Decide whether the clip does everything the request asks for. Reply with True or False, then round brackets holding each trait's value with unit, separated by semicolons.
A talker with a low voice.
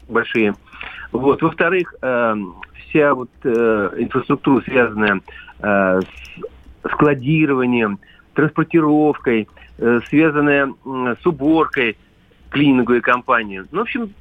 True (125 Hz)